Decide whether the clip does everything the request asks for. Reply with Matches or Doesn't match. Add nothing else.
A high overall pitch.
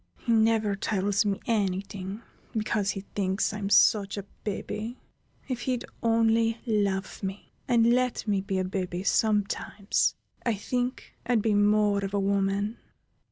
Matches